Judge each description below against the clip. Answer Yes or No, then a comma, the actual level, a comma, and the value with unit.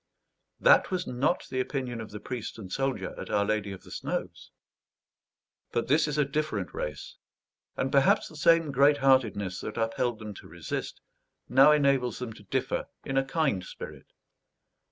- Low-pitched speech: Yes, low, 125 Hz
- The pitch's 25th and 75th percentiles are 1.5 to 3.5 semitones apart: No, average, 4.7 semitones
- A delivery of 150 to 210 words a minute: Yes, average, 170 wpm